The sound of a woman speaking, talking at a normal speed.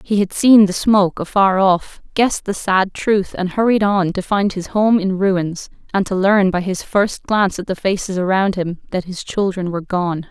No: female; fast, 215 wpm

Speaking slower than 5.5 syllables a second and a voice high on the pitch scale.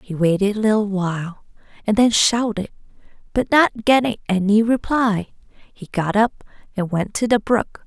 Yes: 4.6 syllables/s; high, 210 Hz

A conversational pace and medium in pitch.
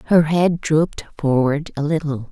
Yes: average, 155 wpm; medium, 150 Hz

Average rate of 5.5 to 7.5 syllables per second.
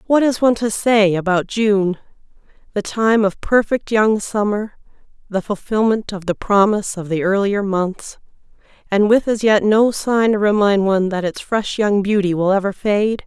No: 4.7 syllables/s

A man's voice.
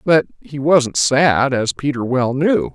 Yes: male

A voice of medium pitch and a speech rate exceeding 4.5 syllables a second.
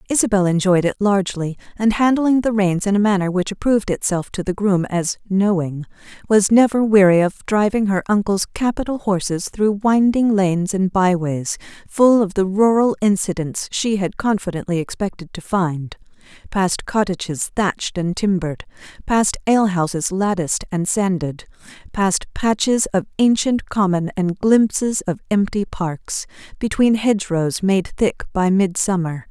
No: high, 195 Hz; 4.7 syllables/s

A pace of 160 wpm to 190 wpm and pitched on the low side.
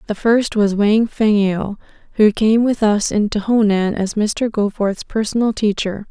No: average, 165 wpm; high, 210 Hz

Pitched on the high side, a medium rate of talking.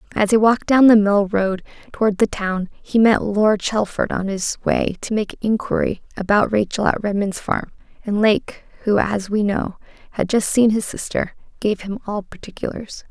Yes: high, 210 Hz; average, 185 wpm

